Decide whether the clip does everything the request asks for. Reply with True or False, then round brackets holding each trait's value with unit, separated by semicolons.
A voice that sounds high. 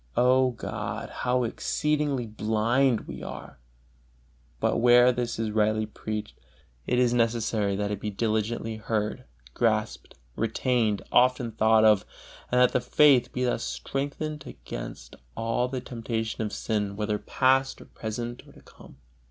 False (115 Hz)